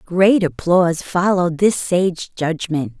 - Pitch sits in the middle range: Yes, medium, 175 Hz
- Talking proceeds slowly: Yes, slow, 120 wpm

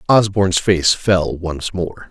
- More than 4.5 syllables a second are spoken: No, 3.6 syllables/s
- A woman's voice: No, male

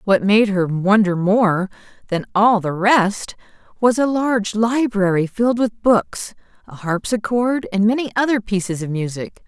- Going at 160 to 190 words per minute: No, average, 150 wpm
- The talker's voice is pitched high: Yes, high, 210 Hz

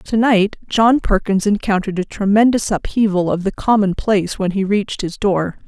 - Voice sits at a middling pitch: No, high, 200 Hz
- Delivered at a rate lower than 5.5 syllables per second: Yes, 5.1 syllables/s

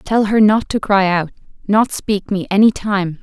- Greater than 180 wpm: Yes, fast, 205 wpm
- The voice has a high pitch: Yes, high, 200 Hz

